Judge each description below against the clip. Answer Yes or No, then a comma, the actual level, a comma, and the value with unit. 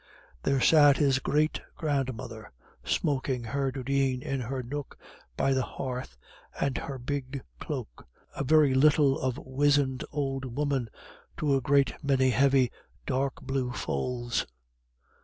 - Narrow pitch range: Yes, narrow, 1.7 semitones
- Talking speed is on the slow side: Yes, slow, 130 wpm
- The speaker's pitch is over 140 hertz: No, low, 135 Hz